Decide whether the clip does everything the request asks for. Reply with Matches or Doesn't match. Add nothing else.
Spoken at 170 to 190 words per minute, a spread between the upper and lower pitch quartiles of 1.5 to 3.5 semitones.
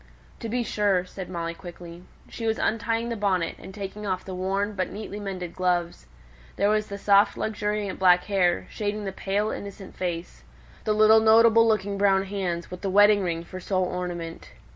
Matches